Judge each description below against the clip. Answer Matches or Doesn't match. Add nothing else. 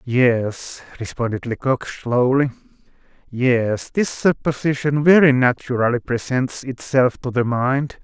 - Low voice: Matches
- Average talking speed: Doesn't match